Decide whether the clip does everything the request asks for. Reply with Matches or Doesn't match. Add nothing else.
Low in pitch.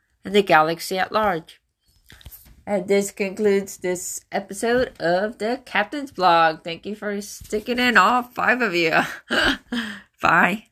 Doesn't match